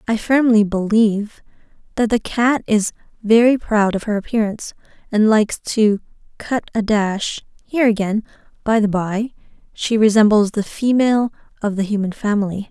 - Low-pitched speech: No, high, 215 Hz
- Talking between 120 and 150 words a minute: Yes, average, 140 wpm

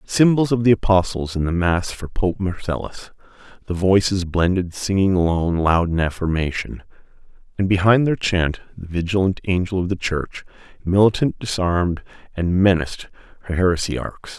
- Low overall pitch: Yes, very low, 95 Hz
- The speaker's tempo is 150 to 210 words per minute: No, average, 140 wpm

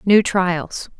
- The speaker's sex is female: Yes, female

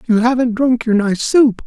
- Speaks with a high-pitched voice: Yes, high, 235 Hz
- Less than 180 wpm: No, fast, 215 wpm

